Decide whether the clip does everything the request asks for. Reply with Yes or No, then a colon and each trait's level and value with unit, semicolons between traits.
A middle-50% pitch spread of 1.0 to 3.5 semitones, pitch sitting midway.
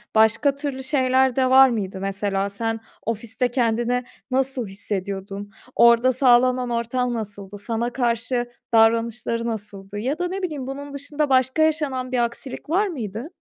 No: average, 3.1 semitones; high, 240 Hz